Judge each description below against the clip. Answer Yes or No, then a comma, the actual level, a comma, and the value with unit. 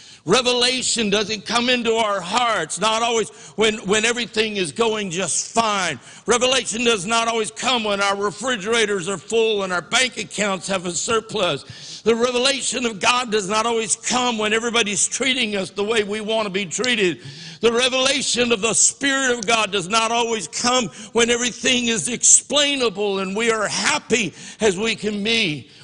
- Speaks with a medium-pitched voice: No, high, 220 Hz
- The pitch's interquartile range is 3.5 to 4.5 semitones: No, average, 2.7 semitones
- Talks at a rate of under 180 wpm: Yes, average, 170 wpm